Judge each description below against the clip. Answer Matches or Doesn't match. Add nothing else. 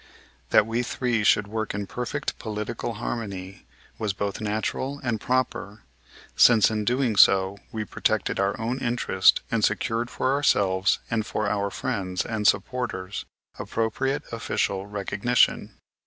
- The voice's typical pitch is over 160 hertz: Doesn't match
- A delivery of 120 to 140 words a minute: Matches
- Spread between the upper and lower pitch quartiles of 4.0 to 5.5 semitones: Doesn't match